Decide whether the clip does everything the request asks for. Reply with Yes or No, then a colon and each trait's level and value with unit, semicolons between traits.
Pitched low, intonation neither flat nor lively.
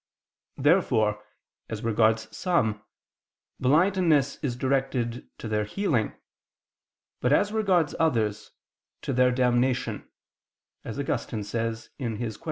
Yes: low, 125 Hz; average, 4.7 semitones